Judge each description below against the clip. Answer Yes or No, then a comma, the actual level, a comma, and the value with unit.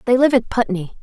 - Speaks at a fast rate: Yes, fast, 235 wpm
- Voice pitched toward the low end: No, high, 235 Hz